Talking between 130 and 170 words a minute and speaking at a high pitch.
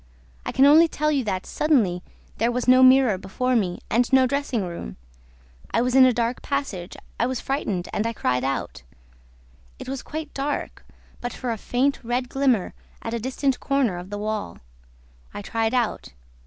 No: average, 180 wpm; high, 245 Hz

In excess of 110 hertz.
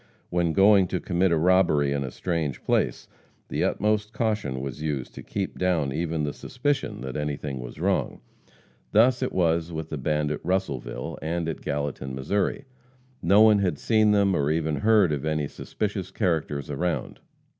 No: very low, 80 Hz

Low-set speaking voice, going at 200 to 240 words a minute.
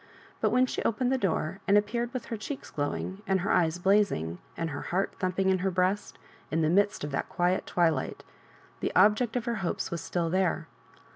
No: high, 190 Hz; fast, 205 wpm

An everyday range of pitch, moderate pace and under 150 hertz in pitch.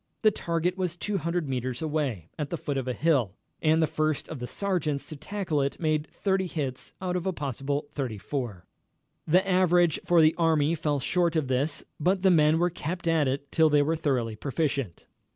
No: average, 3.8 semitones; average, 195 wpm; medium, 155 Hz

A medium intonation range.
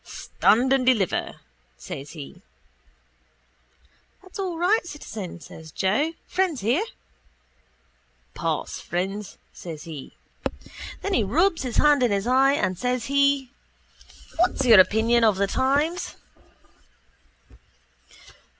No: wide, 7.1 semitones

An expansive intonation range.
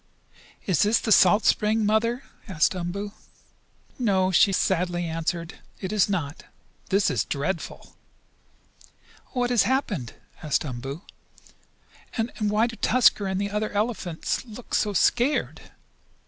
No: average, 4.0 semitones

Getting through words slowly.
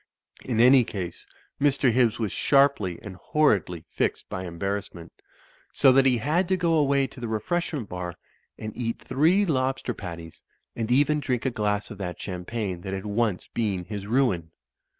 No: average, 170 wpm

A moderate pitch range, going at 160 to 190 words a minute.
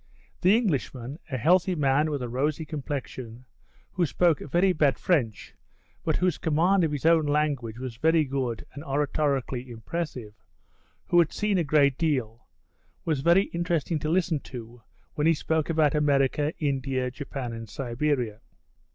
No: average, 4.0 semitones; average, 150 wpm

